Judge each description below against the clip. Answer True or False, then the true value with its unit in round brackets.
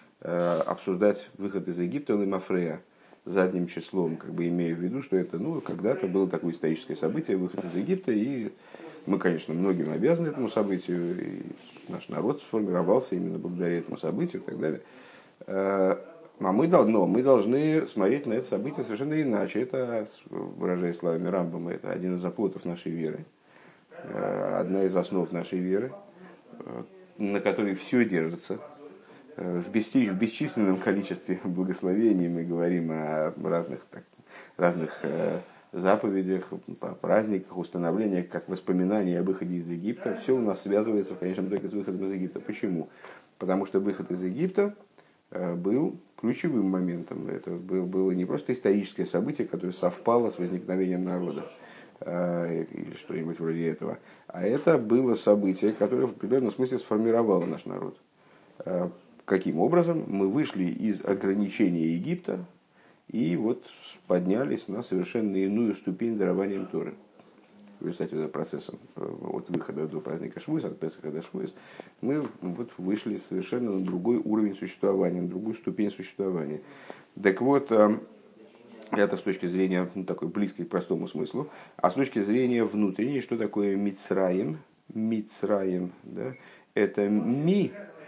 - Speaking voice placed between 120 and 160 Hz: False (95 Hz)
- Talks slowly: False (140 wpm)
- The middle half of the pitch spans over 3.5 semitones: False (3.0 semitones)